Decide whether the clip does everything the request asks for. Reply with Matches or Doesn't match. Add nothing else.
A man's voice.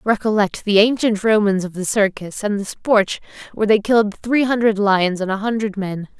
Doesn't match